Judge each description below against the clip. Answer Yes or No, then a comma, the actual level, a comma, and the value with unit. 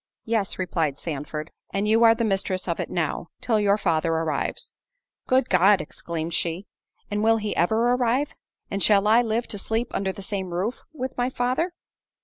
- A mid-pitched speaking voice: No, high, 205 Hz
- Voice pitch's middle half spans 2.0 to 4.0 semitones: No, average, 5.0 semitones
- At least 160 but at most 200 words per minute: Yes, average, 180 wpm